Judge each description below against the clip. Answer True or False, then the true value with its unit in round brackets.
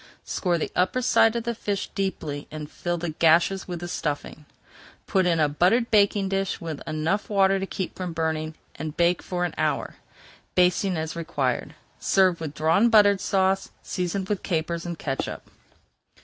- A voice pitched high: False (175 Hz)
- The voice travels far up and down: False (3.4 semitones)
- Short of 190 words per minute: True (170 wpm)